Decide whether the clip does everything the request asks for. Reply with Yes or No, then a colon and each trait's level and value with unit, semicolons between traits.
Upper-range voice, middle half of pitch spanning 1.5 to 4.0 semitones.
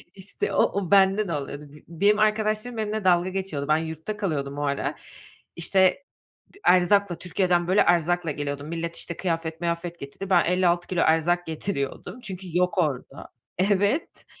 No: medium, 175 Hz; average, 3.4 semitones